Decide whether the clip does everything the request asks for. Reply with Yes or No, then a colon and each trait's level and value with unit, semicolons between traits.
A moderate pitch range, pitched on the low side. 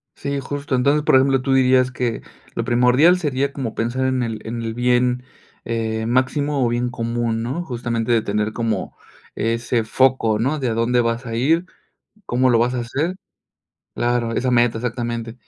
No: narrow, 2.2 semitones; low, 120 Hz